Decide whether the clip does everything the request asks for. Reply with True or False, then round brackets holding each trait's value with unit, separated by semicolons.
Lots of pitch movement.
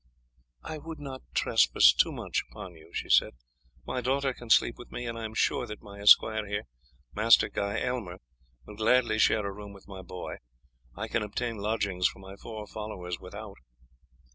False (2.7 semitones)